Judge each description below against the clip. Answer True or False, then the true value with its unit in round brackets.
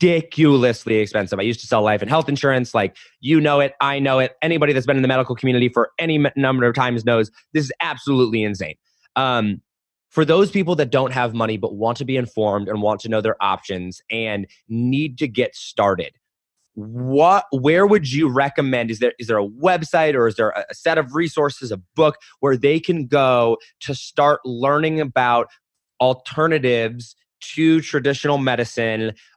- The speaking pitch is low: True (130 Hz)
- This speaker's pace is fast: False (185 wpm)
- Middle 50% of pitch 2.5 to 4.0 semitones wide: False (4.4 semitones)